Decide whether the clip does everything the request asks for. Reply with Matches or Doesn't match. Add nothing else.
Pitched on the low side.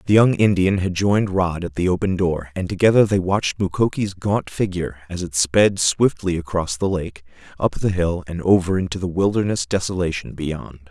Matches